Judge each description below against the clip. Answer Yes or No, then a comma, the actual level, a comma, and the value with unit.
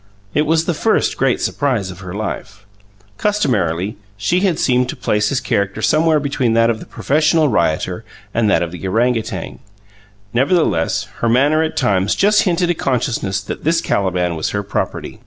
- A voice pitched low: Yes, low, 120 Hz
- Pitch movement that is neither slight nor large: No, wide, 7.8 semitones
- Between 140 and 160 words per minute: No, average, 175 wpm